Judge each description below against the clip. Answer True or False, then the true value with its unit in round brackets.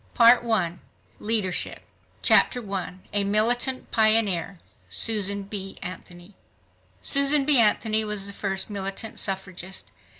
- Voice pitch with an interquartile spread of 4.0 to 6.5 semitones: False (2.9 semitones)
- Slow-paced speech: True (105 wpm)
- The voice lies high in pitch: True (200 Hz)